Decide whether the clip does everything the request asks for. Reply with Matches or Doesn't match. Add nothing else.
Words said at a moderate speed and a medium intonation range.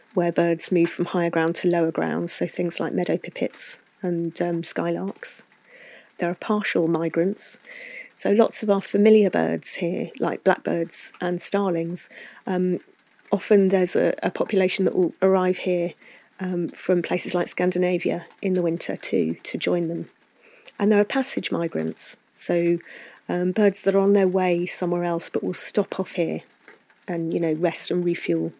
Doesn't match